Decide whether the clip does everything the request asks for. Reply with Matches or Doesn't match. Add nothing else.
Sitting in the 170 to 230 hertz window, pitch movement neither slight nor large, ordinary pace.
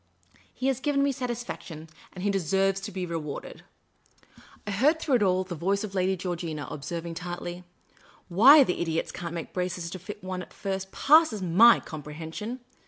Matches